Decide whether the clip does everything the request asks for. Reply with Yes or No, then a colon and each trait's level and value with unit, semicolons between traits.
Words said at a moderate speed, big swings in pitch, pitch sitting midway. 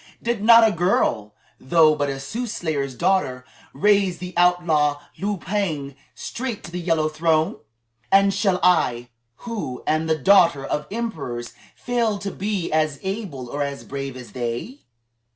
Yes: average, 150 wpm; wide, 6.0 semitones; medium, 165 Hz